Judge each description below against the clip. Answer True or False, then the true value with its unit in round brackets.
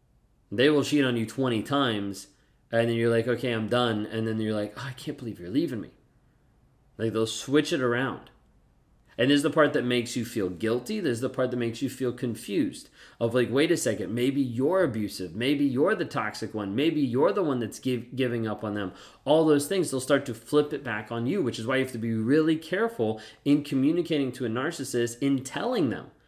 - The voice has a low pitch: True (125 Hz)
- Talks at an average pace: False (230 wpm)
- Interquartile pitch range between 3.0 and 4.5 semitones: True (3.9 semitones)